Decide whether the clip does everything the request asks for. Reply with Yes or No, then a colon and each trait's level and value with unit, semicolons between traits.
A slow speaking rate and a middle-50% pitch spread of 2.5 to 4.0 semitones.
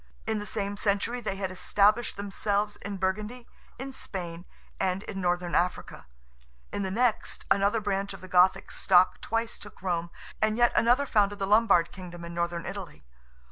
No: average, 170 wpm; average, 2.8 semitones